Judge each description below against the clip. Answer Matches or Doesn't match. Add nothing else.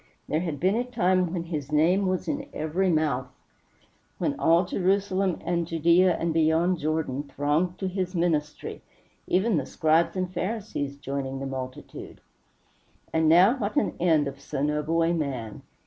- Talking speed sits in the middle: Matches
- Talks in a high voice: Doesn't match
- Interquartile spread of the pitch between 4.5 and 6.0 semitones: Doesn't match